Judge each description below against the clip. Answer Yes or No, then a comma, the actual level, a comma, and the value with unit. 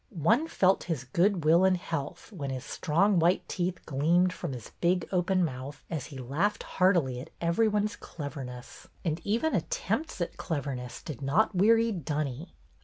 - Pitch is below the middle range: No, medium, 170 Hz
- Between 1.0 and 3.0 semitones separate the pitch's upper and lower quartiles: No, average, 5.2 semitones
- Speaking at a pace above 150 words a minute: Yes, average, 165 wpm